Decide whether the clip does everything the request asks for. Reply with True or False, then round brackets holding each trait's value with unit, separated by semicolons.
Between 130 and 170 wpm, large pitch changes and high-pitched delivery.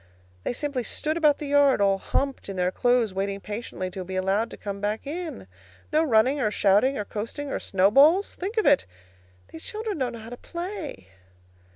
False (195 wpm; 6.7 semitones; 245 Hz)